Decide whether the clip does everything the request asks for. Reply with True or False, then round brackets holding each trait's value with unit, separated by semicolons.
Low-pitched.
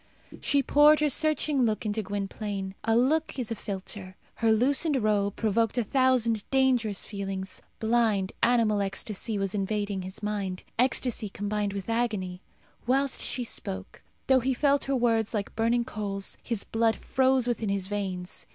False (220 Hz)